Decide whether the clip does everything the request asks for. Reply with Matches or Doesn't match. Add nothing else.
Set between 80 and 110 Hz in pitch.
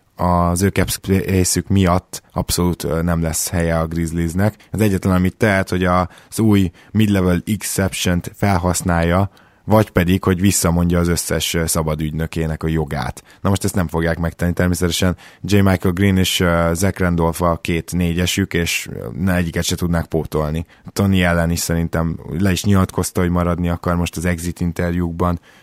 Matches